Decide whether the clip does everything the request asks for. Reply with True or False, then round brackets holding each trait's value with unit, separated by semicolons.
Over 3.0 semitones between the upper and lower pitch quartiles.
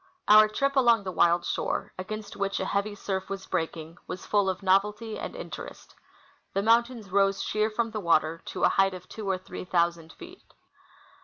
False (2.7 semitones)